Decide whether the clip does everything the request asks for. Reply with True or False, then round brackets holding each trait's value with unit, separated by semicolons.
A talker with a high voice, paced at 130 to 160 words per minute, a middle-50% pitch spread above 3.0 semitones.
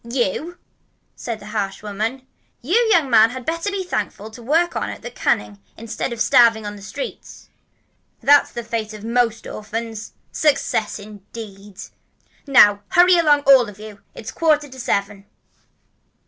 True (230 Hz; 155 wpm; 4.9 semitones)